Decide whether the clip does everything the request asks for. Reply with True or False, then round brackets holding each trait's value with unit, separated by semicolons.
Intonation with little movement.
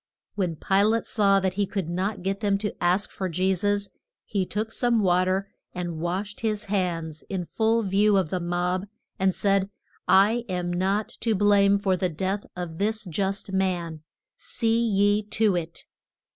True (2.3 semitones)